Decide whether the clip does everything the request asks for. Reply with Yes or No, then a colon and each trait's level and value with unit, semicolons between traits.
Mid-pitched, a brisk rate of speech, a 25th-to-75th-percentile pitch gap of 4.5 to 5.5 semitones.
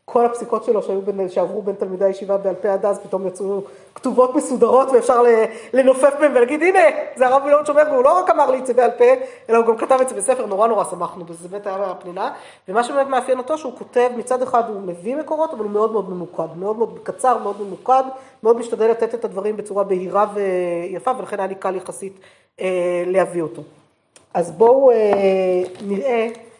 No: high, 225 Hz; fast, 200 wpm; average, 4.9 semitones